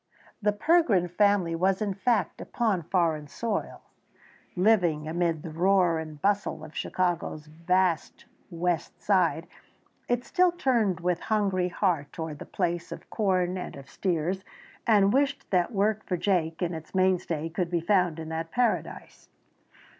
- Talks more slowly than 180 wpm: Yes, average, 145 wpm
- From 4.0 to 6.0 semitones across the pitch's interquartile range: No, average, 3.5 semitones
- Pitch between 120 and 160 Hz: No, medium, 180 Hz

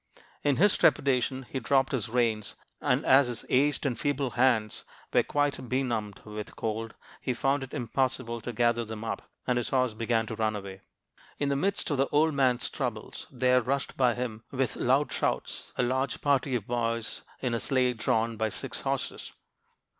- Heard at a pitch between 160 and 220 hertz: No, low, 125 Hz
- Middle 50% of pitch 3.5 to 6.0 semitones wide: No, average, 3.0 semitones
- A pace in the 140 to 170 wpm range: No, average, 185 wpm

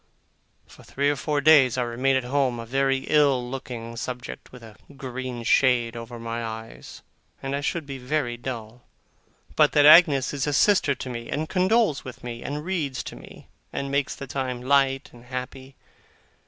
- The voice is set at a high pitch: No, low, 130 Hz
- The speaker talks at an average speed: Yes, average, 180 wpm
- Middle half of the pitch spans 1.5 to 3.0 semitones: Yes, average, 2.7 semitones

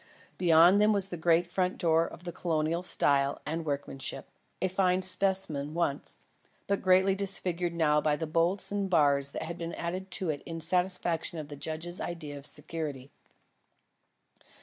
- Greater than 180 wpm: No, average, 160 wpm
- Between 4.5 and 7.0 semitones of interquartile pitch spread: No, average, 3.2 semitones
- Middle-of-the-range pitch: Yes, medium, 170 Hz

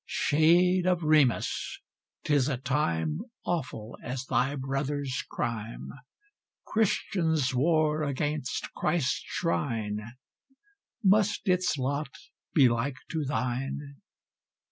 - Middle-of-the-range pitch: Yes, medium, 145 Hz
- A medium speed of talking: No, slow, 95 wpm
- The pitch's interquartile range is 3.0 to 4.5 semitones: Yes, average, 3.9 semitones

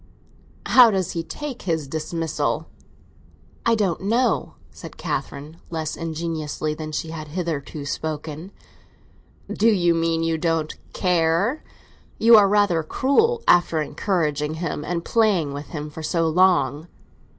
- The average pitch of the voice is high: No, medium, 165 Hz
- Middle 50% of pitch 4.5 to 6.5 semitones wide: No, average, 3.5 semitones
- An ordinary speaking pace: No, slow, 130 wpm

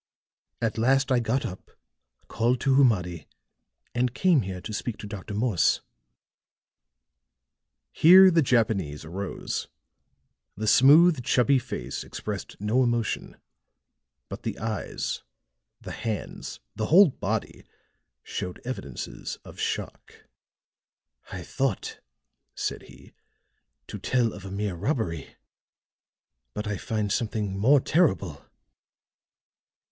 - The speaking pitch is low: Yes, low, 115 Hz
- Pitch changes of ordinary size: Yes, average, 4.6 semitones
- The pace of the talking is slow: Yes, slow, 110 wpm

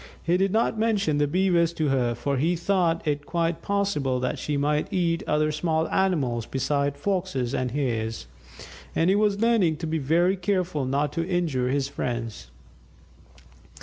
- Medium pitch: Yes, medium, 160 Hz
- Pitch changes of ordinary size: Yes, average, 5.0 semitones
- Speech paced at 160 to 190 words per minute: Yes, average, 165 wpm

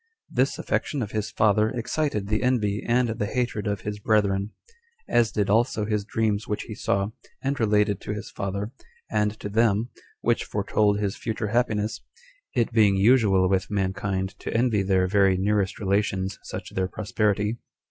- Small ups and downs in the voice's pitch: Yes, narrow, 2.0 semitones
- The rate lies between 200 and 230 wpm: No, average, 165 wpm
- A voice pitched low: Yes, low, 105 Hz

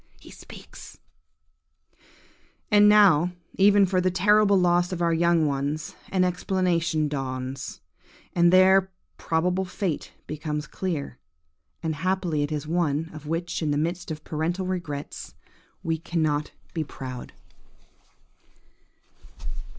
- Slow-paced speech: Yes, slow, 120 wpm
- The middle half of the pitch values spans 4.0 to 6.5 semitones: No, average, 3.4 semitones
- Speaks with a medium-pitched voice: Yes, medium, 170 Hz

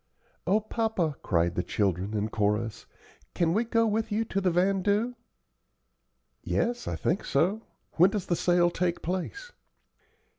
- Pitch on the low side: No, medium, 180 Hz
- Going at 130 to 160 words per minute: Yes, average, 145 wpm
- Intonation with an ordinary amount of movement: No, wide, 7.9 semitones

